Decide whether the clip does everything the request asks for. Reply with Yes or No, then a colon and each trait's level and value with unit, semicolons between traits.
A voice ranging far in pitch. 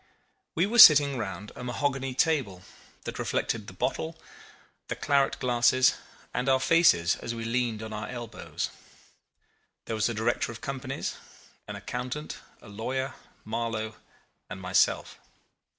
No: average, 3.5 semitones